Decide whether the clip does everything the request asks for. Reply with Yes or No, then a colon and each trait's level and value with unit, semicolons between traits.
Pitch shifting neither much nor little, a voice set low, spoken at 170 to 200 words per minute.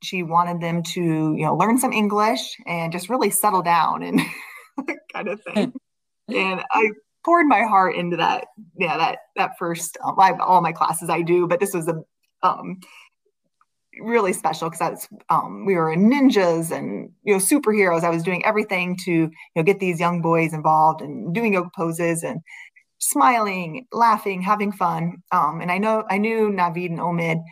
No: average, 4.1 semitones; medium, 180 Hz; average, 180 wpm